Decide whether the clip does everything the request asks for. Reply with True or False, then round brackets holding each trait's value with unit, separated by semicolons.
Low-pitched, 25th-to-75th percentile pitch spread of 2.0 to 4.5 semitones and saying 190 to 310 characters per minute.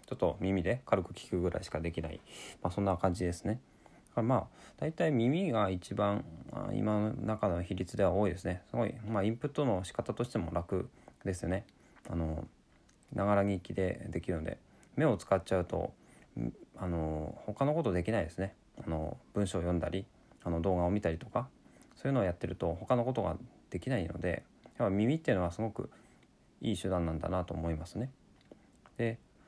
False (95 Hz; 4.1 semitones; 345 characters per minute)